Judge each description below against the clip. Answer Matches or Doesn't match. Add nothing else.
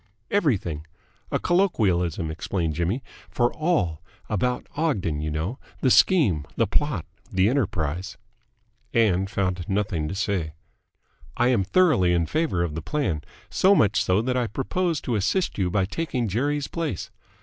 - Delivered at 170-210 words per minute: Doesn't match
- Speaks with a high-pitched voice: Doesn't match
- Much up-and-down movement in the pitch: Matches